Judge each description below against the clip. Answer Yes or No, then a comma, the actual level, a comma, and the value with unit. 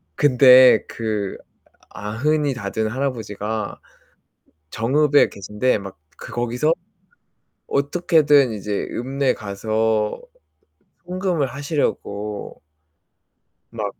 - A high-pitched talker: No, low, 120 Hz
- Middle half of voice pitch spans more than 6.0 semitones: No, average, 5.1 semitones